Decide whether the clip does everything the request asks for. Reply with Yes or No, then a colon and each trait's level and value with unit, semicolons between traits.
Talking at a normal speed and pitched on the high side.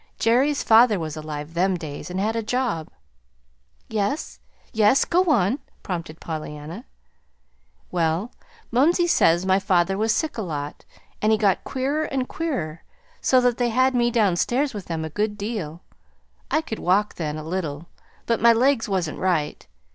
Yes: average, 160 wpm; high, 205 Hz